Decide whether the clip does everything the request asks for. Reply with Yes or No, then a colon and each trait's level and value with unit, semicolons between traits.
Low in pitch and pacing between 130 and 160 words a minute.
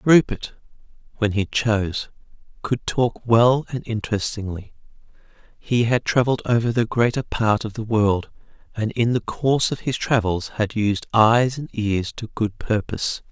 Yes: low, 115 Hz; average, 155 wpm